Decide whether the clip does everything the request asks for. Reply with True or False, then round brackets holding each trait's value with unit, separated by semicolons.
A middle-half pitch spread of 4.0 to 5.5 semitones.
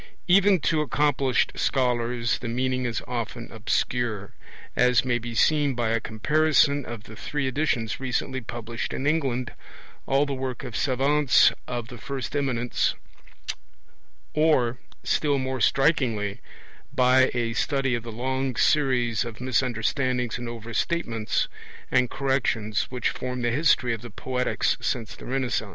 False (2.5 semitones)